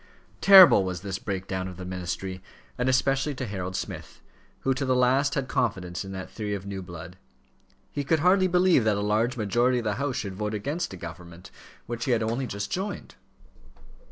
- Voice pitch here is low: Yes, low, 110 Hz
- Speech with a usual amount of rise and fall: No, wide, 5.9 semitones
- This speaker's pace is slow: No, fast, 205 wpm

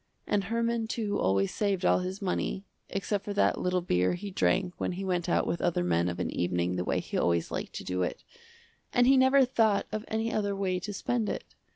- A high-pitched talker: Yes, high, 195 Hz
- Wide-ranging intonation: No, average, 4.2 semitones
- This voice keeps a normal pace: No, fast, 225 wpm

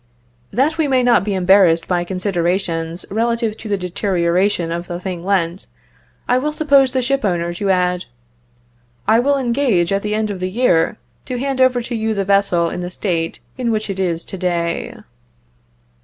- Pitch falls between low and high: No, high, 195 Hz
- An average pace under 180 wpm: No, average, 185 wpm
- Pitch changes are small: No, average, 5.2 semitones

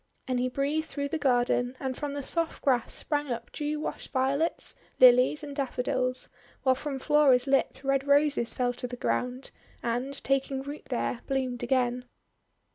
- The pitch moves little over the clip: Yes, narrow, 2.3 semitones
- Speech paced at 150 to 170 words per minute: Yes, average, 165 wpm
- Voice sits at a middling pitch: No, very high, 265 Hz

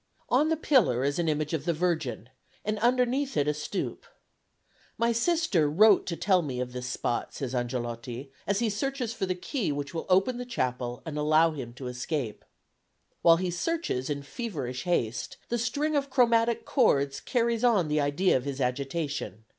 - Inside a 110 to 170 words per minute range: No, average, 180 wpm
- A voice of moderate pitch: Yes, medium, 165 Hz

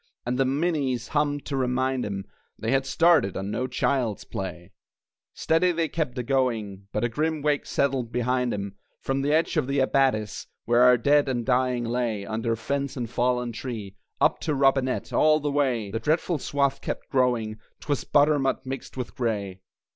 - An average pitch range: Yes, average, 3.5 semitones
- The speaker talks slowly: No, average, 175 wpm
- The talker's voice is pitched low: Yes, low, 130 Hz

